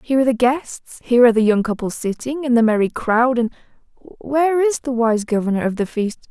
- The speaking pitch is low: No, high, 245 Hz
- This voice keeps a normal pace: No, fast, 220 wpm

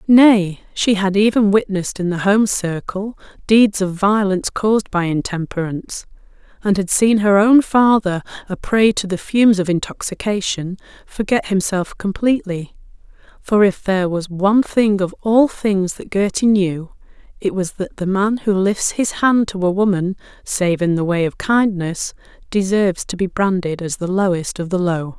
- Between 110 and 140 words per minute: No, average, 170 wpm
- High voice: Yes, high, 195 Hz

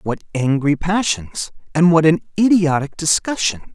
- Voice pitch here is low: No, medium, 160 Hz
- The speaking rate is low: Yes, slow, 110 wpm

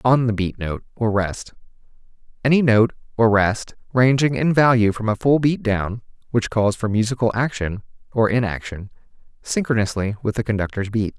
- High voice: No, low, 115 Hz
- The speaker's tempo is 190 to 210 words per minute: No, average, 160 wpm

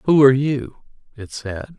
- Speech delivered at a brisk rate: No, average, 170 wpm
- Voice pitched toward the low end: Yes, low, 125 Hz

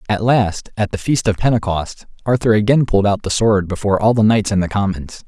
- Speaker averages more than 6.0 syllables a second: No, 5.7 syllables/s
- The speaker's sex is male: Yes, male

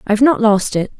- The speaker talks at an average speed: No, fast, 240 wpm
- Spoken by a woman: Yes, female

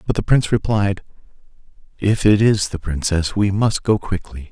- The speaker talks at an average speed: Yes, average, 175 wpm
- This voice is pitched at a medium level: No, low, 100 Hz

